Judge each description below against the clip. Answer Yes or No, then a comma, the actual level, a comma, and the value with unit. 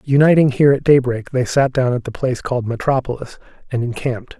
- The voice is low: Yes, low, 130 Hz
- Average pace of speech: Yes, average, 190 wpm